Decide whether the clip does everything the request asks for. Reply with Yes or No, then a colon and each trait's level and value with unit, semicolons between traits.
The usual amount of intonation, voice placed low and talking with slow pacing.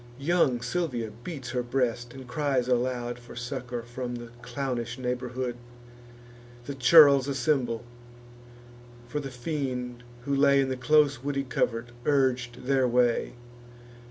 No: narrow, 2.2 semitones; low, 125 Hz; slow, 130 wpm